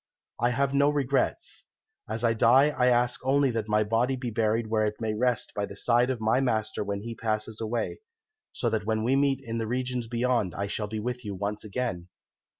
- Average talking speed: No, fast, 215 wpm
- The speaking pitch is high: No, low, 115 Hz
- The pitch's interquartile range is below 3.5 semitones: Yes, average, 2.7 semitones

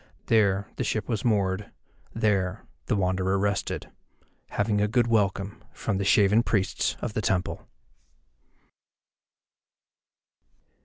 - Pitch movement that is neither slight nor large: No, narrow, 2.0 semitones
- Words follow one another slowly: Yes, slow, 110 wpm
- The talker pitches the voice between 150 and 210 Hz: No, low, 100 Hz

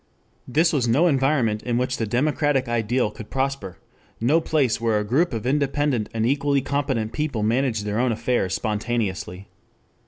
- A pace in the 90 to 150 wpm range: No, average, 160 wpm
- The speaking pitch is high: No, low, 125 Hz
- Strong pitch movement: No, average, 4.1 semitones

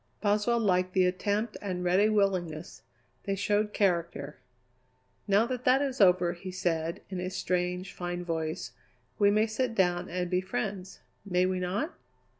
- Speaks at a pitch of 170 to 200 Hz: Yes, medium, 185 Hz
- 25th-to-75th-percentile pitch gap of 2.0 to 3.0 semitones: Yes, average, 2.7 semitones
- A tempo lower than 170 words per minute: Yes, average, 155 wpm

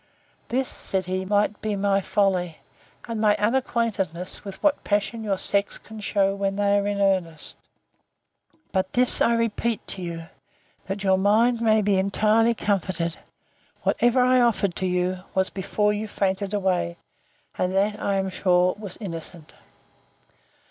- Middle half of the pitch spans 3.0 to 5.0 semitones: No, narrow, 2.4 semitones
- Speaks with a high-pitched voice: Yes, high, 200 Hz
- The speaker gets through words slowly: No, average, 150 wpm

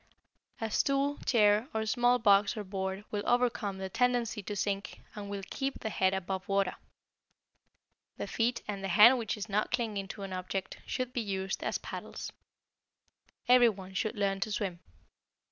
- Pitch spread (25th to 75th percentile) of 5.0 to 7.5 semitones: No, average, 3.4 semitones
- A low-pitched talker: No, high, 210 Hz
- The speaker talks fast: No, average, 170 wpm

